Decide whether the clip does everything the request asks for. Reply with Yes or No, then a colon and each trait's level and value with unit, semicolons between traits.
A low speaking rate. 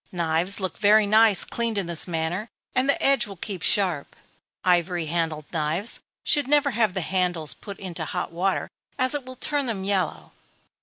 No: average, 175 wpm